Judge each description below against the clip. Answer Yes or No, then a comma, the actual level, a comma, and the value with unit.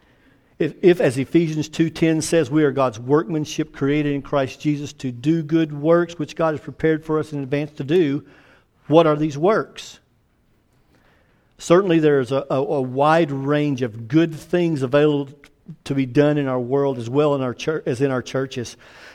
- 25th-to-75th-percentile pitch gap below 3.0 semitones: Yes, narrow, 2.5 semitones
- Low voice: No, medium, 145 Hz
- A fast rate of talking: No, average, 185 wpm